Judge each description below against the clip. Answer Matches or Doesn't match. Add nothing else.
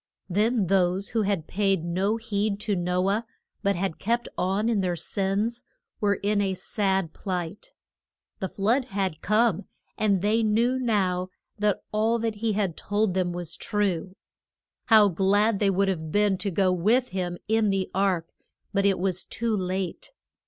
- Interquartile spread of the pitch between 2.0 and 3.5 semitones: Matches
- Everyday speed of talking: Matches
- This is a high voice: Matches